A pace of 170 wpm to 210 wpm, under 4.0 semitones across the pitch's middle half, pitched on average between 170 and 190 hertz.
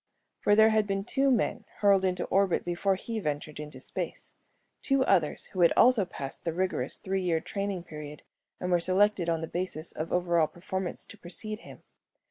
Yes: average, 190 wpm; average, 3.2 semitones; medium, 185 Hz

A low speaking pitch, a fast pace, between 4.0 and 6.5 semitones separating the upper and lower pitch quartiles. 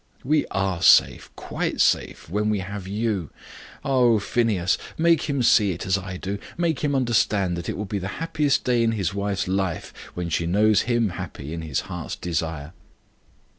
No: low, 100 Hz; average, 180 wpm; average, 4.5 semitones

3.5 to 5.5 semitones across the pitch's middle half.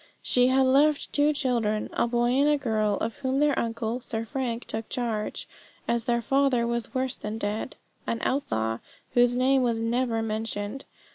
No: average, 2.7 semitones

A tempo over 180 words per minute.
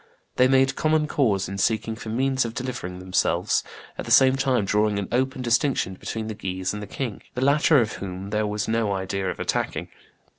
Yes: average, 200 wpm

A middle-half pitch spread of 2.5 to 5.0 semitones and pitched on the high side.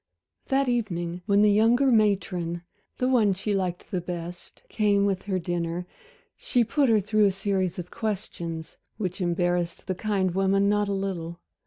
Yes: average, 3.2 semitones; high, 195 Hz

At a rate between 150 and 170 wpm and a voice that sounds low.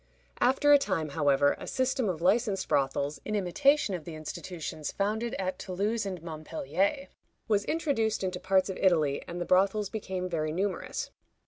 No: average, 160 wpm; high, 190 Hz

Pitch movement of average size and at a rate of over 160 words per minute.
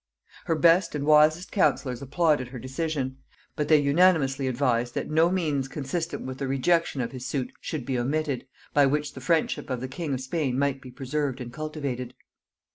Yes: average, 3.1 semitones; average, 185 wpm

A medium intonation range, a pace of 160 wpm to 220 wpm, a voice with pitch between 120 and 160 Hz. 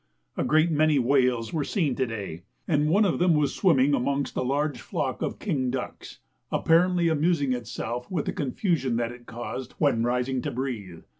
Yes: average, 4.2 semitones; average, 180 wpm; low, 135 Hz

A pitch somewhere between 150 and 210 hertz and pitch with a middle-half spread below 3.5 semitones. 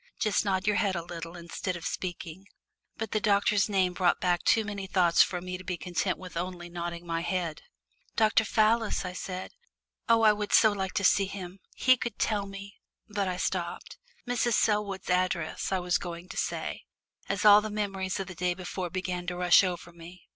Yes: medium, 185 Hz; narrow, 2.5 semitones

